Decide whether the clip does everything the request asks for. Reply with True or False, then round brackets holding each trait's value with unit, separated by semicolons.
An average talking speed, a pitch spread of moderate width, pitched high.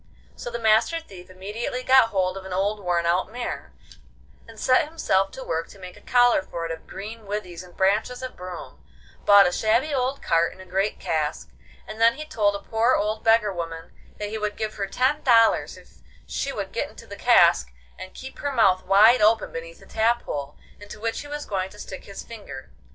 False (215 wpm; 4.0 semitones; 210 Hz)